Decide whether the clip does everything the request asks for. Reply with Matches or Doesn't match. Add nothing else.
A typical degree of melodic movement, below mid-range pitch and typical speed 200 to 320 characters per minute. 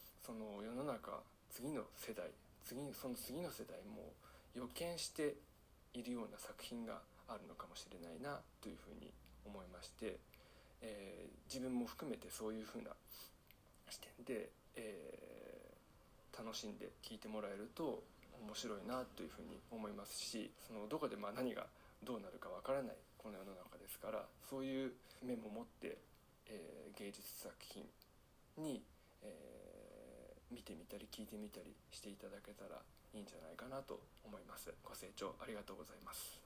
Matches